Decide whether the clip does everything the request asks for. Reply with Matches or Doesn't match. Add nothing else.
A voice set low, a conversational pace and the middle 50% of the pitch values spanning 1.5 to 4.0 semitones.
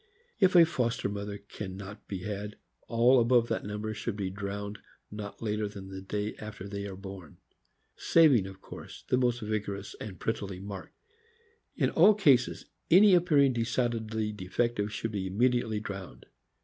Matches